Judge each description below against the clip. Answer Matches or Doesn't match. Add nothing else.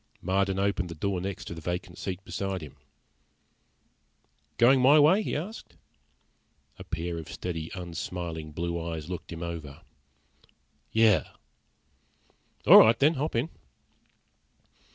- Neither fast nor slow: Doesn't match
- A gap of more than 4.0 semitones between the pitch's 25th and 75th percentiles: Matches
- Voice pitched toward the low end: Matches